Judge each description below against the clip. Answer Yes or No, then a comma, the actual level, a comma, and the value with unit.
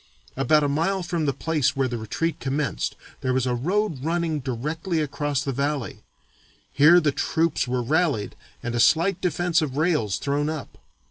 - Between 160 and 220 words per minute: Yes, average, 175 wpm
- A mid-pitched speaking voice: Yes, medium, 145 Hz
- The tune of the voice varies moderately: Yes, average, 3.9 semitones